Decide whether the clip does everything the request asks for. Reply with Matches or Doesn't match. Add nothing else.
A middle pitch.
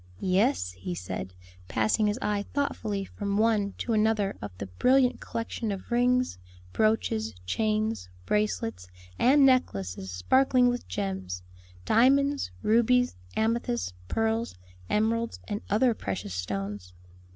Doesn't match